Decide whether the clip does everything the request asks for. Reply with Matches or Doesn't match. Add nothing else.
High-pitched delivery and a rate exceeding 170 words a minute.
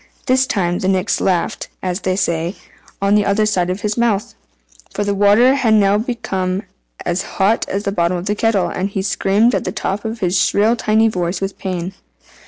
Matches